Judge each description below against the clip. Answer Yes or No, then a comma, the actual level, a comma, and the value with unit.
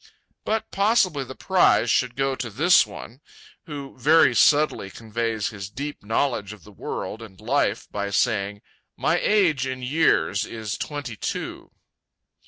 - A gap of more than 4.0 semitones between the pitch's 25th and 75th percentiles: Yes, wide, 5.6 semitones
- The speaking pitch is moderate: No, low, 125 Hz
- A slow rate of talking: No, average, 145 wpm